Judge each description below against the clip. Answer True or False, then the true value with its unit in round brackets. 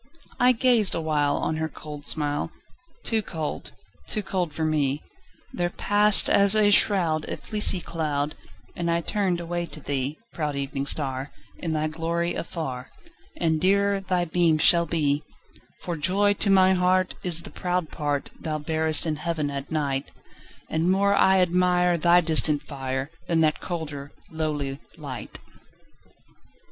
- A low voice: False (160 Hz)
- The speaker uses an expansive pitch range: False (3.5 semitones)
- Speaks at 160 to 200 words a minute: False (150 wpm)